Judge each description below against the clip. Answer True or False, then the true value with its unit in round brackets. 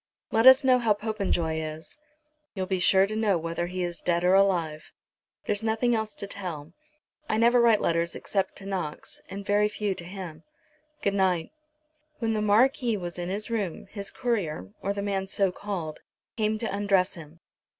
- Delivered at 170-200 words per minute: True (180 wpm)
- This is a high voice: True (195 Hz)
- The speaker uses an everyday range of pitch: True (3.7 semitones)